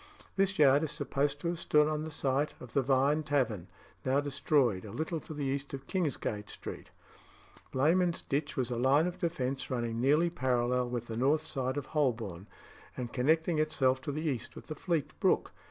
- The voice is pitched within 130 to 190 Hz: Yes, medium, 140 Hz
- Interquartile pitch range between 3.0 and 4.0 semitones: Yes, average, 3.4 semitones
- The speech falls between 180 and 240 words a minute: Yes, average, 190 wpm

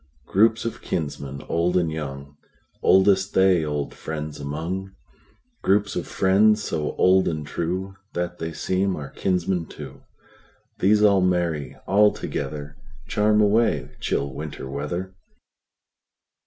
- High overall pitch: No, very low, 90 Hz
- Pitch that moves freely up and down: No, average, 4.3 semitones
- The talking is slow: Yes, slow, 105 wpm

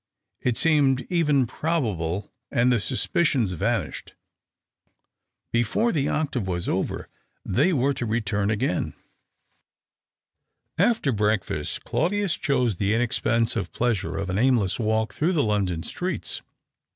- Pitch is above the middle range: No, low, 120 Hz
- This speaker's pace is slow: Yes, slow, 125 wpm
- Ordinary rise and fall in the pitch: No, wide, 5.7 semitones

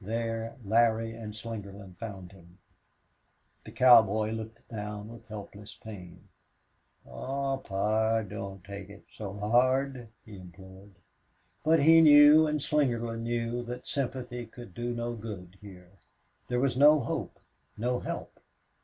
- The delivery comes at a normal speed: No, slow, 130 wpm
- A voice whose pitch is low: Yes, low, 115 Hz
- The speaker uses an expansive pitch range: No, average, 3.4 semitones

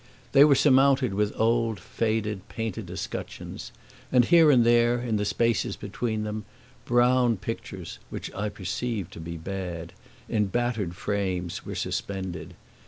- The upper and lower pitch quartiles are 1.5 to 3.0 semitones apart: No, average, 3.8 semitones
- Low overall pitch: Yes, low, 110 Hz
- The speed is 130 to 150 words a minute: Yes, average, 140 wpm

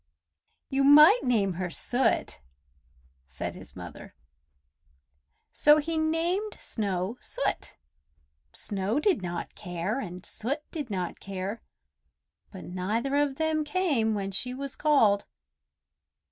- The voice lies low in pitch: No, high, 245 Hz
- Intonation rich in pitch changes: Yes, wide, 7.4 semitones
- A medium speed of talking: No, slow, 115 wpm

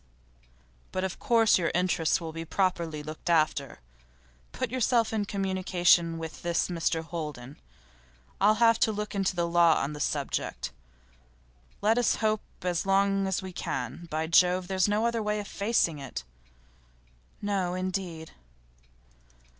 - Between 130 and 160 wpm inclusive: Yes, average, 145 wpm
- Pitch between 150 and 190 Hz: Yes, medium, 185 Hz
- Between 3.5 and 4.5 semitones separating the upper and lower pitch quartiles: Yes, average, 3.8 semitones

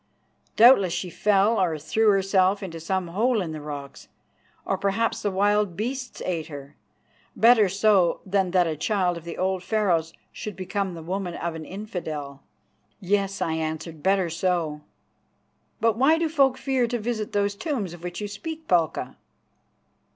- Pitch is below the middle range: No, high, 190 Hz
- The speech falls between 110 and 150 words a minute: No, average, 165 wpm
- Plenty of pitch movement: No, average, 4.1 semitones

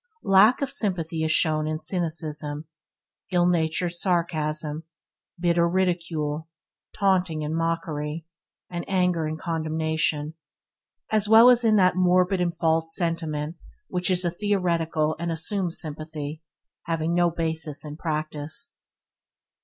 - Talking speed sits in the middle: No, slow, 120 wpm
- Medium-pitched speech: Yes, medium, 165 Hz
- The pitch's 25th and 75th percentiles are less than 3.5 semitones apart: Yes, narrow, 2.4 semitones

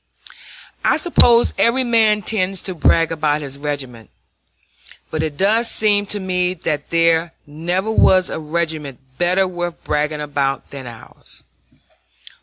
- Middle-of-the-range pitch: Yes, medium, 170 Hz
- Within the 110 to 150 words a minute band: Yes, slow, 135 wpm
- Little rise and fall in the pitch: No, average, 4.5 semitones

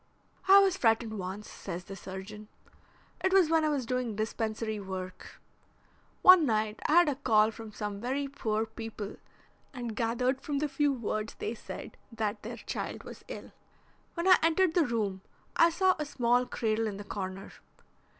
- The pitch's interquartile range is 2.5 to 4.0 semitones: No, average, 5.3 semitones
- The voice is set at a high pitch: Yes, high, 225 Hz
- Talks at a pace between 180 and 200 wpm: No, average, 170 wpm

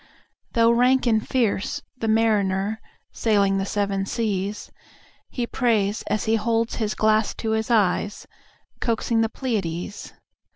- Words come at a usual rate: No, slow, 115 wpm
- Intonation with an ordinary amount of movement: No, narrow, 2.2 semitones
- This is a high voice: Yes, high, 220 Hz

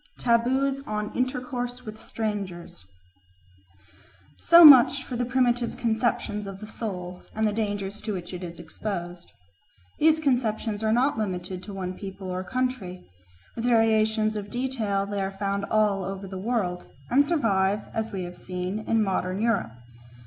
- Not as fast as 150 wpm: No, average, 155 wpm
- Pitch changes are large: No, average, 4.0 semitones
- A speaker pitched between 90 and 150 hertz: No, high, 215 Hz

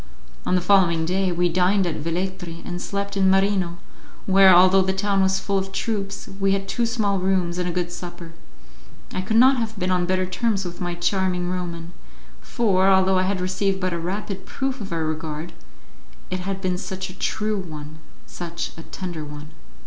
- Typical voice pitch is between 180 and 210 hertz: Yes, medium, 185 Hz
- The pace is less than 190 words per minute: No, average, 195 wpm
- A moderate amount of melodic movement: No, narrow, 1.8 semitones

